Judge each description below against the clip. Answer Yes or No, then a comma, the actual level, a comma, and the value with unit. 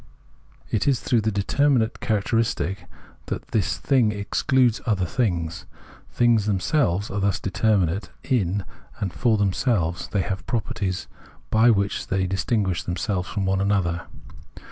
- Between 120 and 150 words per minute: Yes, average, 145 wpm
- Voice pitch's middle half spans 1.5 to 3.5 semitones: Yes, average, 3.2 semitones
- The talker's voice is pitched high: No, low, 100 Hz